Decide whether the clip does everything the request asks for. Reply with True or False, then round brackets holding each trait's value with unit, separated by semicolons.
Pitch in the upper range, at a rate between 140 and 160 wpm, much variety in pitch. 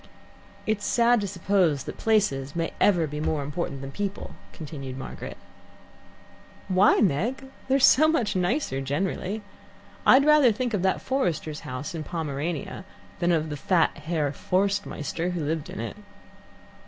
False (175 Hz; 150 wpm; 5.8 semitones)